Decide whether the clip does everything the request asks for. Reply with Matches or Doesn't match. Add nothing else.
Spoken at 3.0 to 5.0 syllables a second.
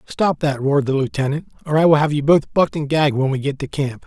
Doesn't match